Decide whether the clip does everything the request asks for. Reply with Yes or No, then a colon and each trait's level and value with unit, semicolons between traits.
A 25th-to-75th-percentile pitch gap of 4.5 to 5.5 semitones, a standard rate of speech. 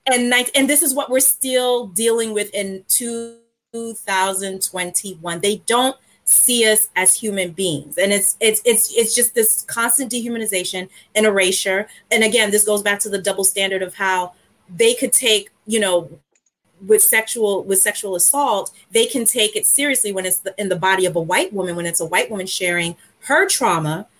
No: average, 3.8 semitones; average, 185 wpm